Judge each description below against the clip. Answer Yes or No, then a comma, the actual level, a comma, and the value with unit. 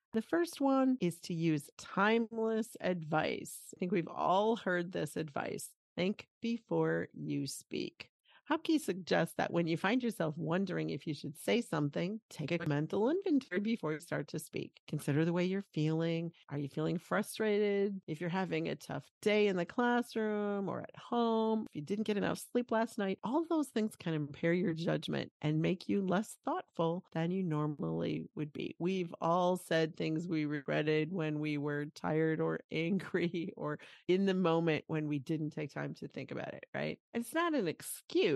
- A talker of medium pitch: Yes, medium, 175 Hz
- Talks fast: No, average, 185 wpm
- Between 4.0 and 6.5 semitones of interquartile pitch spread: Yes, average, 5.2 semitones